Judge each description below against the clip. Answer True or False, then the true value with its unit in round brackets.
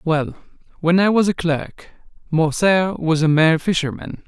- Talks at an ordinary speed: True (155 wpm)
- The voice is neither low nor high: True (165 Hz)